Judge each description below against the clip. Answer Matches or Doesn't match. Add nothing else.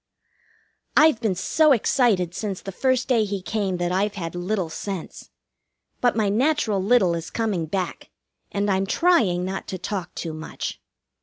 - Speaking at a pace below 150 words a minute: Doesn't match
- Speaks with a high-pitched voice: Matches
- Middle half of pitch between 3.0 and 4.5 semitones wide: Matches